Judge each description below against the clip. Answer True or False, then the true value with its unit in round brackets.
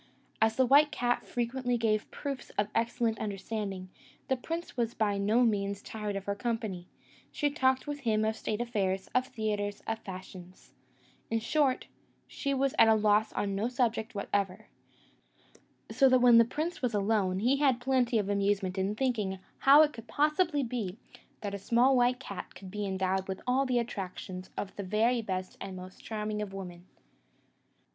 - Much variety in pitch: False (3.9 semitones)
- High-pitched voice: True (220 Hz)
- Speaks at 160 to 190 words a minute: True (180 wpm)